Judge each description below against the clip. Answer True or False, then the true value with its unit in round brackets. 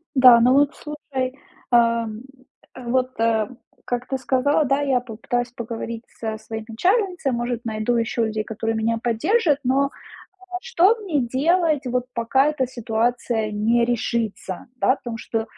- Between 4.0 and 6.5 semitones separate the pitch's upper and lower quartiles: False (3.2 semitones)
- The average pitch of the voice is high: True (245 Hz)